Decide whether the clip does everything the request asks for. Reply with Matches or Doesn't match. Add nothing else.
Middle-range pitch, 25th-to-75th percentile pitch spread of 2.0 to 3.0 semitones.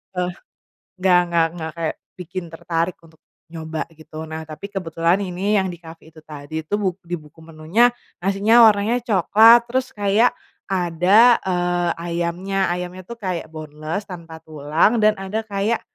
Doesn't match